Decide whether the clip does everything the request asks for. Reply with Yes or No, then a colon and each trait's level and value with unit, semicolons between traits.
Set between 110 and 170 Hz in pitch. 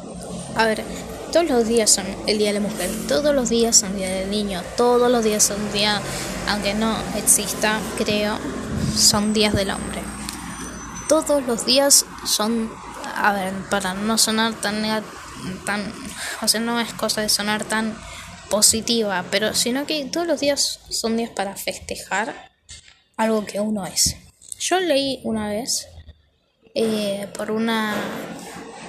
No: high, 215 Hz